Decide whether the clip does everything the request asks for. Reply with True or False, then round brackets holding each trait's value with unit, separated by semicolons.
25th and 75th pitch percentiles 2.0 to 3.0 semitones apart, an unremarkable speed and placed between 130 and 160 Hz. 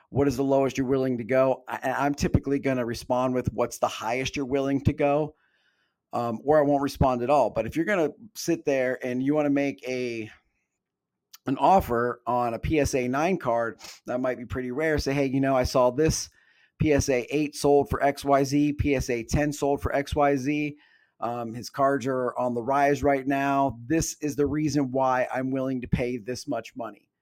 False (2.4 semitones; 210 wpm; 135 Hz)